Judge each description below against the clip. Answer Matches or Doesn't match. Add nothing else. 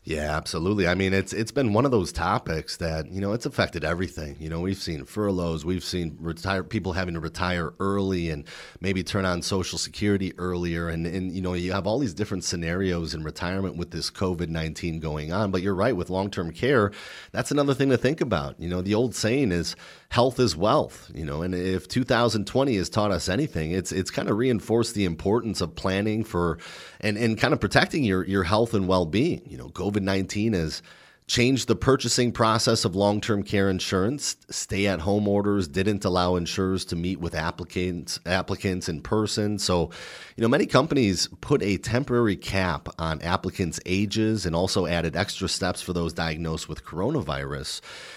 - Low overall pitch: Matches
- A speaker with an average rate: Matches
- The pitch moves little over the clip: Doesn't match